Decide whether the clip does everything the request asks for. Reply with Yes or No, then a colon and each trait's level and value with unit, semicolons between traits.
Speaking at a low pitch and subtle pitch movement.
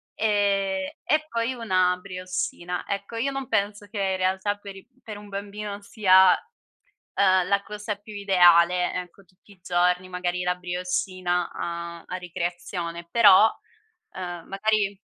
No: high, 190 Hz; narrow, 2.3 semitones